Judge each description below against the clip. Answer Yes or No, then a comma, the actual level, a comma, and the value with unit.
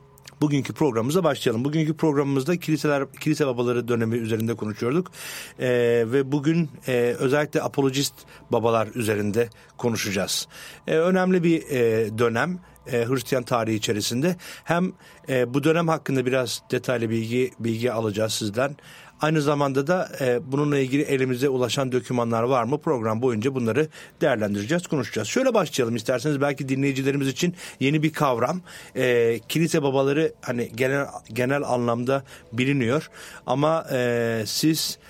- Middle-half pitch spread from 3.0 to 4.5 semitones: Yes, average, 4.2 semitones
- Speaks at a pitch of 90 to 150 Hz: Yes, low, 135 Hz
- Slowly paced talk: Yes, slow, 130 wpm